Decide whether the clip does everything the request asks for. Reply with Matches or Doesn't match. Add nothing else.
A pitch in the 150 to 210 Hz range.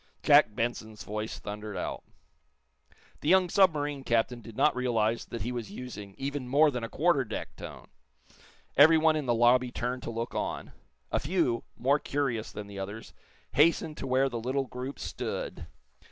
Doesn't match